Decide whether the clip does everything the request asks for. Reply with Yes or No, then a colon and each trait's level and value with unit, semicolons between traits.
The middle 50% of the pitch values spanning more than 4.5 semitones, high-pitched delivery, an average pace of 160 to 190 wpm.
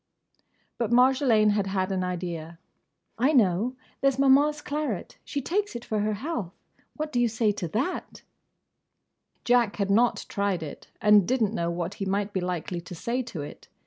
Yes: wide, 5.4 semitones; high, 215 Hz; average, 180 wpm